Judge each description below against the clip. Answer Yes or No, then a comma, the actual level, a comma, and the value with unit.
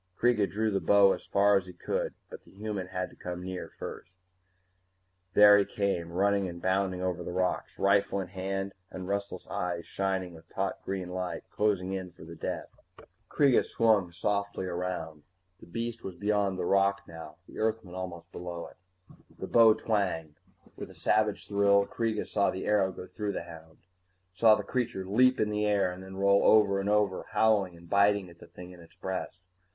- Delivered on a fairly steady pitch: Yes, narrow, 2.2 semitones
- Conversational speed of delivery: Yes, average, 190 wpm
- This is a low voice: Yes, very low, 95 Hz